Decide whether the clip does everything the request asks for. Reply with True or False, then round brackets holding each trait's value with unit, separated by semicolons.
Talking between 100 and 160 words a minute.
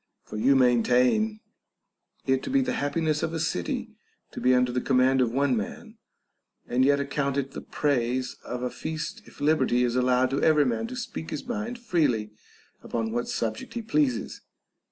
False (175 wpm)